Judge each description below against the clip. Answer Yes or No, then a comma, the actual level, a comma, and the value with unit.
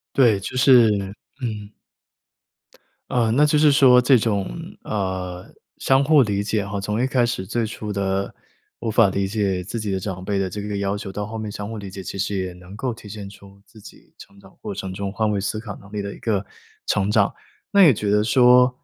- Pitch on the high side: No, low, 105 Hz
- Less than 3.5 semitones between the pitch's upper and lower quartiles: Yes, average, 3.0 semitones